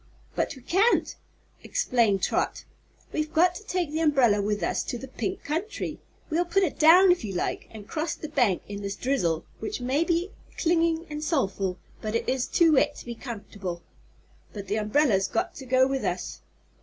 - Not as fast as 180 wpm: No, average, 185 wpm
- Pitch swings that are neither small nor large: No, wide, 7.8 semitones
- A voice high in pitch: Yes, very high, 270 Hz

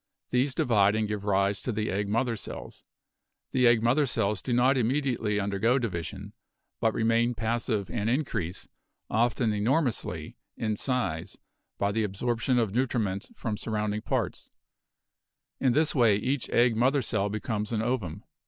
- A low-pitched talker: Yes, low, 115 Hz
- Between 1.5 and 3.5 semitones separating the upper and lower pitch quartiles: Yes, average, 3.2 semitones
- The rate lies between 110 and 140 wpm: No, average, 155 wpm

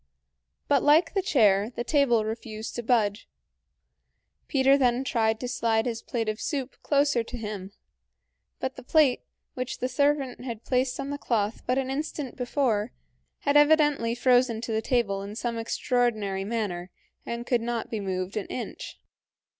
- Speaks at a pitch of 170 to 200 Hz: No, high, 240 Hz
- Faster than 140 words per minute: Yes, average, 160 wpm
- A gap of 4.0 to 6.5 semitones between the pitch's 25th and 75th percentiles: No, average, 3.3 semitones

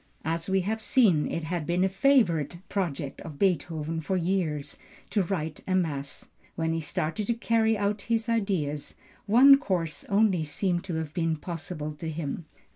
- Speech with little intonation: No, average, 4.2 semitones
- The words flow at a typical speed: Yes, average, 170 wpm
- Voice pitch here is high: No, medium, 175 Hz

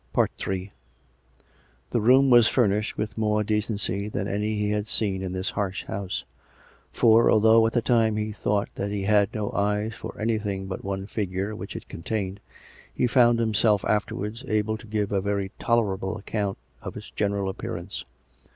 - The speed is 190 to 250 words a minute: No, average, 170 wpm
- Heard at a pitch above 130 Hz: No, low, 105 Hz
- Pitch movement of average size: No, narrow, 1.8 semitones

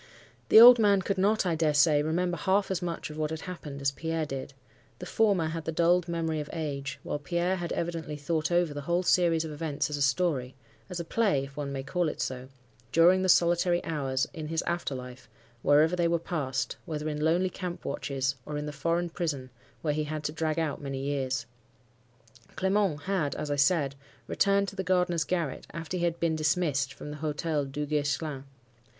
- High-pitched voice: No, medium, 160 Hz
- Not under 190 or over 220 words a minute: Yes, average, 200 wpm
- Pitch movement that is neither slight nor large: Yes, average, 3.3 semitones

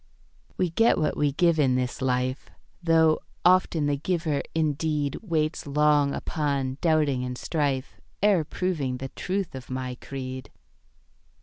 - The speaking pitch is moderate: Yes, medium, 150 Hz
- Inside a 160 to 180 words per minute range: No, slow, 135 wpm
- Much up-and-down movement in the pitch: No, average, 3.7 semitones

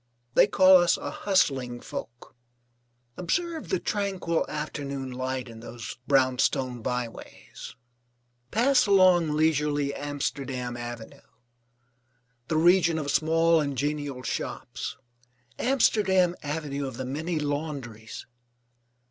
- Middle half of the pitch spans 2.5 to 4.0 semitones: No, average, 5.2 semitones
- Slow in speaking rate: Yes, slow, 105 wpm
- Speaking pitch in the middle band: Yes, medium, 145 Hz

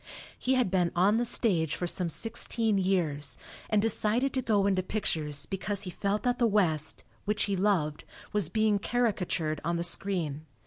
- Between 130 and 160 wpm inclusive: No, average, 175 wpm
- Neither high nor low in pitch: No, high, 195 Hz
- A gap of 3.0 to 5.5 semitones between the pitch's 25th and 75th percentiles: Yes, average, 4.1 semitones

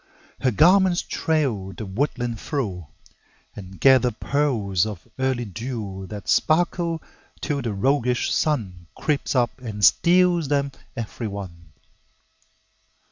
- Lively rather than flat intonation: Yes, wide, 6.4 semitones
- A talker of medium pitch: No, low, 120 Hz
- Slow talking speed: Yes, slow, 115 wpm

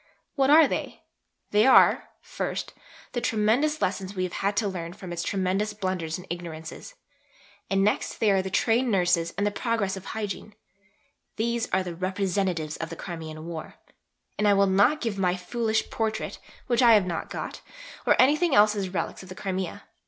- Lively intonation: No, average, 3.4 semitones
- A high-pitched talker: Yes, high, 195 Hz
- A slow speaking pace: No, average, 180 wpm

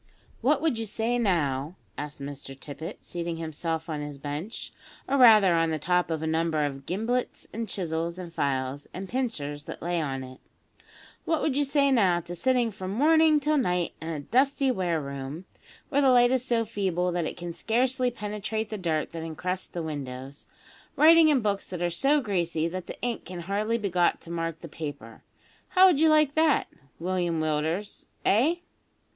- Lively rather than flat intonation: Yes, wide, 7.2 semitones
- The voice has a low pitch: No, medium, 180 Hz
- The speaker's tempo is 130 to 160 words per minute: No, average, 190 wpm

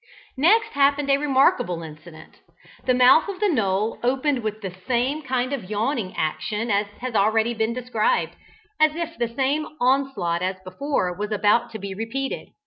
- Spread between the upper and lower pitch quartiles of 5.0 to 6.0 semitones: Yes, wide, 5.4 semitones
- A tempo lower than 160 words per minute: No, average, 165 wpm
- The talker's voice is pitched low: No, high, 235 Hz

